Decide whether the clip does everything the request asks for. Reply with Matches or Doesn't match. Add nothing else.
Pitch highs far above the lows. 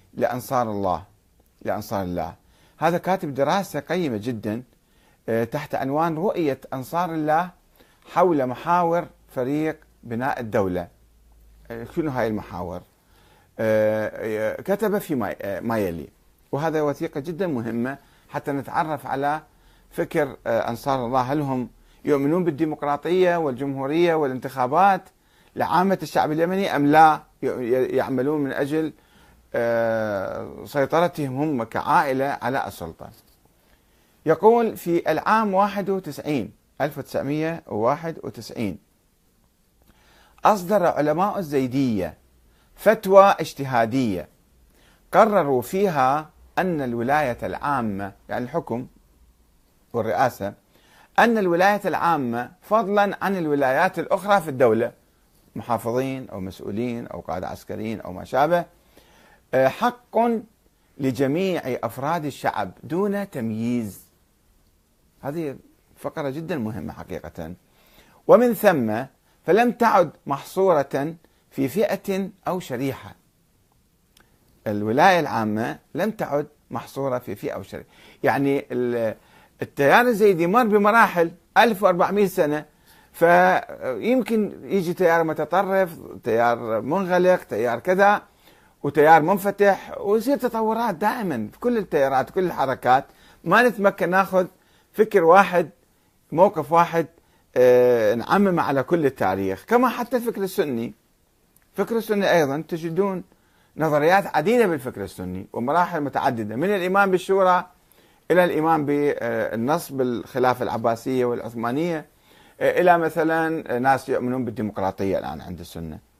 Matches